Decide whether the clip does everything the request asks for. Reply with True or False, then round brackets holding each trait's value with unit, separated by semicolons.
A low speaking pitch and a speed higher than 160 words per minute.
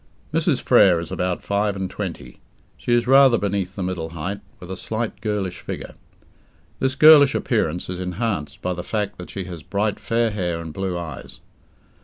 True (95 Hz; 180 wpm)